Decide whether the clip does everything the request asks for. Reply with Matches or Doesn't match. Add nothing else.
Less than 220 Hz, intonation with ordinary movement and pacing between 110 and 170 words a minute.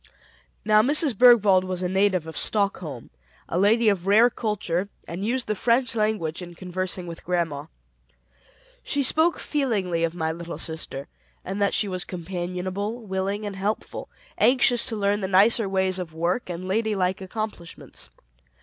Matches